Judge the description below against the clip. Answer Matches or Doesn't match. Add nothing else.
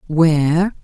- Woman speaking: Matches